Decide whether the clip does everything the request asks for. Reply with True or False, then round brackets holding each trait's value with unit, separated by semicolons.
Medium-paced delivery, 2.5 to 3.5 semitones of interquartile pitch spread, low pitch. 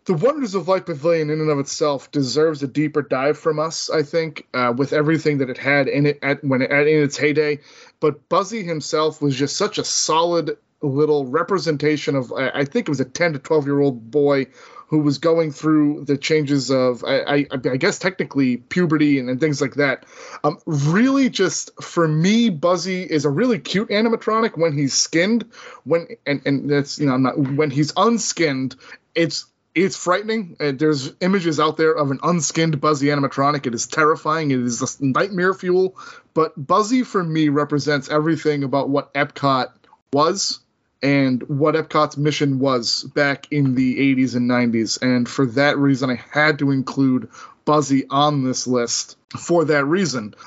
False (180 wpm; 2.9 semitones; 150 Hz)